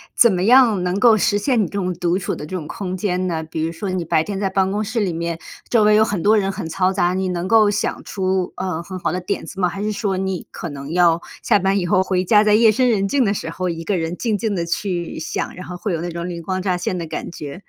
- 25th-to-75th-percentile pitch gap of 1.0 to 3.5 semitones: Yes, average, 2.8 semitones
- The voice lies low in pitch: No, medium, 185 Hz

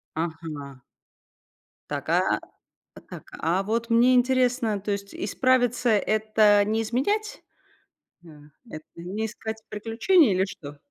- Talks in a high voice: Yes, high, 215 Hz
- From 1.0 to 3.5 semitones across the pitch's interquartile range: No, average, 4.3 semitones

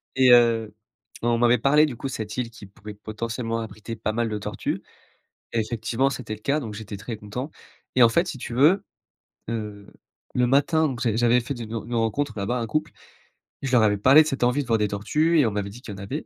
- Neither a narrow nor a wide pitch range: Yes, average, 3.4 semitones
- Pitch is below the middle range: Yes, low, 115 Hz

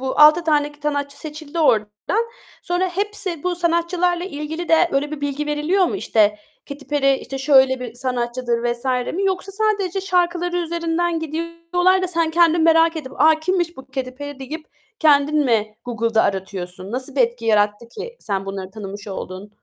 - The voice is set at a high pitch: Yes, very high, 295 Hz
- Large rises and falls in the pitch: Yes, wide, 5.9 semitones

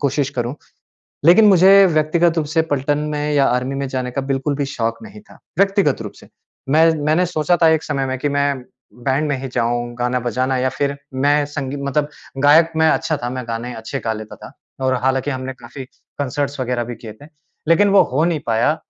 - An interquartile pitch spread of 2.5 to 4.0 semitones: Yes, average, 3.4 semitones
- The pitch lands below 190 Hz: Yes, medium, 140 Hz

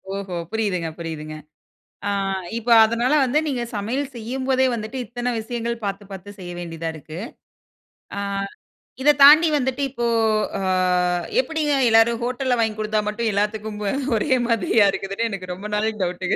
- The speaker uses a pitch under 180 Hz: No, high, 220 Hz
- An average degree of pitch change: Yes, average, 3.9 semitones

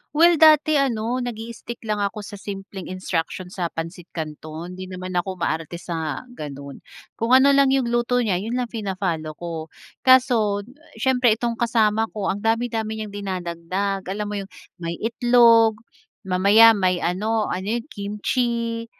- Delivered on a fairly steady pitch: No, average, 4.3 semitones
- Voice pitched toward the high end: Yes, high, 210 Hz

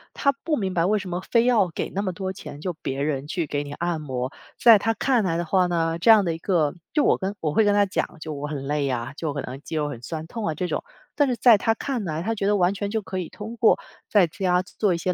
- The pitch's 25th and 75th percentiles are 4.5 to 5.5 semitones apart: Yes, average, 5.0 semitones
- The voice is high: No, medium, 180 Hz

